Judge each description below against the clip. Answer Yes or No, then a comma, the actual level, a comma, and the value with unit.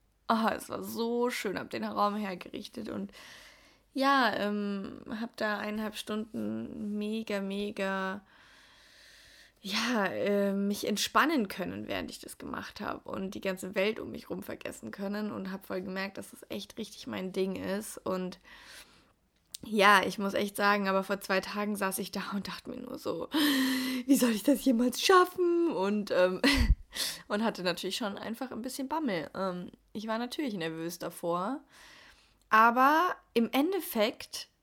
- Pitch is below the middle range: No, high, 210 Hz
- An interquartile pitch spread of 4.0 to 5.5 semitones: Yes, average, 4.3 semitones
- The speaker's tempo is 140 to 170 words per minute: Yes, average, 160 wpm